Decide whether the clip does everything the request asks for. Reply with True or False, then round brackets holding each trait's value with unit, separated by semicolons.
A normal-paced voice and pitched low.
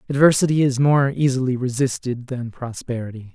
False (125 wpm; 130 Hz)